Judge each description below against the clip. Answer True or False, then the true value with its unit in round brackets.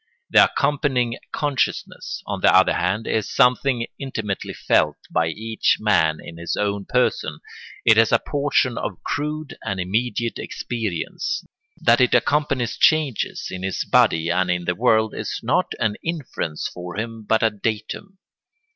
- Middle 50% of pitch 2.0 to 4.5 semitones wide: False (4.9 semitones)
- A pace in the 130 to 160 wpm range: True (150 wpm)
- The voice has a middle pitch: False (110 Hz)